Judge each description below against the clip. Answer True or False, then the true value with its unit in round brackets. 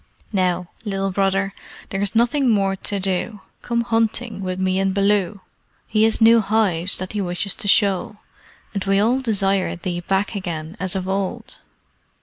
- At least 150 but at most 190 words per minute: True (165 wpm)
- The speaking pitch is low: False (195 Hz)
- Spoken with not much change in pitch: True (2.3 semitones)